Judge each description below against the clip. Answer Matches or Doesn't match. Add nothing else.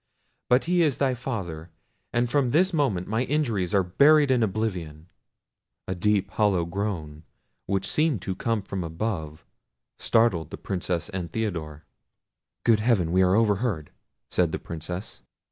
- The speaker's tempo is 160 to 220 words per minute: Doesn't match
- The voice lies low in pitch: Matches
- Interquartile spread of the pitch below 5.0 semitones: Doesn't match